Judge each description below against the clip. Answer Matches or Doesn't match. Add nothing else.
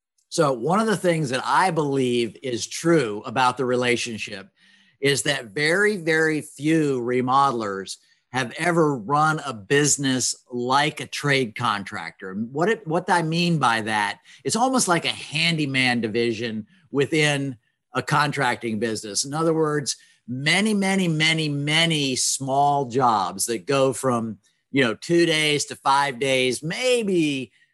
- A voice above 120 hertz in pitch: Matches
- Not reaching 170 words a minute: Matches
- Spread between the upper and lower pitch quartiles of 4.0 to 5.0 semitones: Matches